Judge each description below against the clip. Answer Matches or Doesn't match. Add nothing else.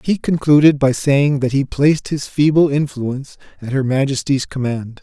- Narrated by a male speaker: Matches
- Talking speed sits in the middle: Matches